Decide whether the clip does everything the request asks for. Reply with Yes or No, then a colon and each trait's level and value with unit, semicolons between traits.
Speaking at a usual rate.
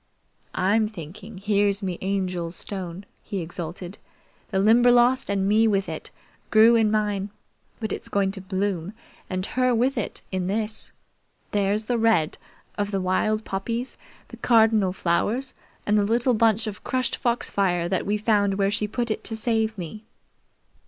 Yes: average, 160 wpm